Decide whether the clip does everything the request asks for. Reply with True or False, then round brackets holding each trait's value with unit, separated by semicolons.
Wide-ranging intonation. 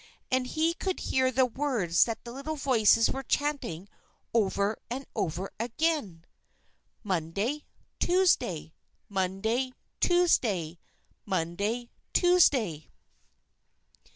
True (6.6 semitones)